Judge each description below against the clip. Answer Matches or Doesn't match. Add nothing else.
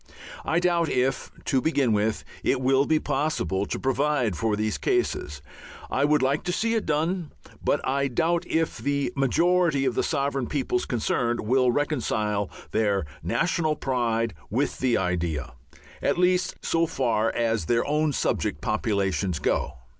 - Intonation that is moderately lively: Doesn't match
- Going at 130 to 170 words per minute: Matches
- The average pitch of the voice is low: Matches